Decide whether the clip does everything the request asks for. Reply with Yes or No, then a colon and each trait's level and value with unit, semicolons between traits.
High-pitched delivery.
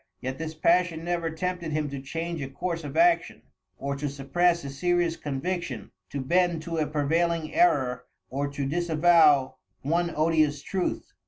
No: medium, 160 Hz